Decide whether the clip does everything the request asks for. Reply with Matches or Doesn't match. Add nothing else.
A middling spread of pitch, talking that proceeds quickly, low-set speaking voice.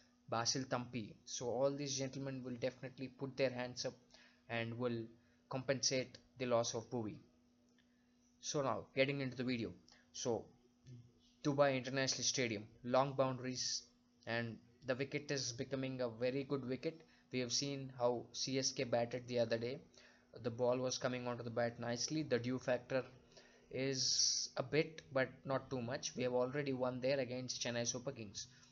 Doesn't match